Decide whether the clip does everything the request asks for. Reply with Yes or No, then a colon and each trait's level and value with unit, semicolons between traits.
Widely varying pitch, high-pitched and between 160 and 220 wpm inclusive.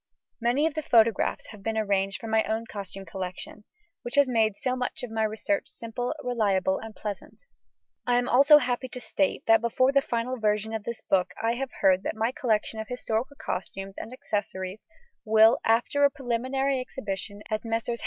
No: average, 3.0 semitones; high, 225 Hz; average, 185 wpm